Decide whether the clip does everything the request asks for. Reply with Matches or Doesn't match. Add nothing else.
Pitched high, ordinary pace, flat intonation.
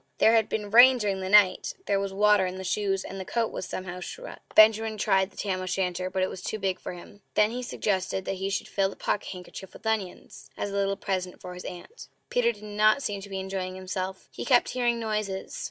Doesn't match